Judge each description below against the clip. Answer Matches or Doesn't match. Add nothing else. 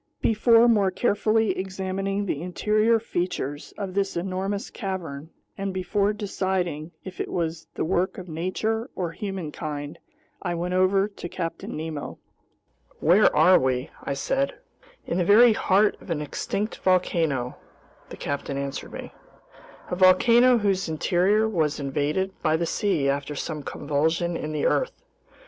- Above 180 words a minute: Doesn't match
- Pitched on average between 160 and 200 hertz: Matches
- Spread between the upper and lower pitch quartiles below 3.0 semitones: Doesn't match